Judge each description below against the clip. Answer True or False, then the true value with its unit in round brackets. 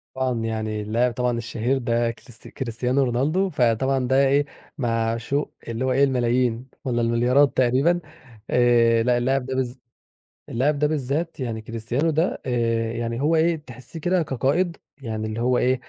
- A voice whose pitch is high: False (125 Hz)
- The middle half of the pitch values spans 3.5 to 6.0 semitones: False (2.9 semitones)